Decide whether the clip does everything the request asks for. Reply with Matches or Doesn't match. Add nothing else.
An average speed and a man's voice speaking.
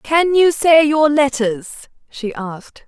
Doesn't match